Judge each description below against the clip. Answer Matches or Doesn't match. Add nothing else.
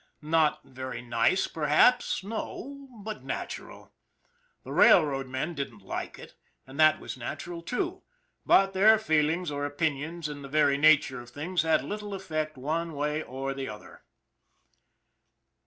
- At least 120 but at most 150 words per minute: Matches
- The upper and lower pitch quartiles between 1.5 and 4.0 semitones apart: Doesn't match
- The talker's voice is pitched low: Doesn't match